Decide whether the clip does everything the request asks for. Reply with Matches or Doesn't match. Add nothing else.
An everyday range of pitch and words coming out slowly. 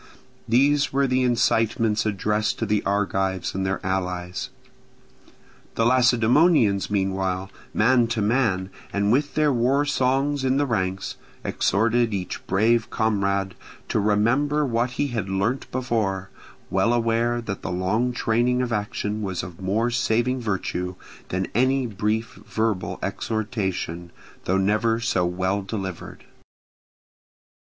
Matches